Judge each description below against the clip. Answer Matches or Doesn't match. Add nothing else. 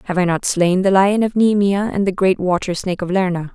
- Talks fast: Matches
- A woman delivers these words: Matches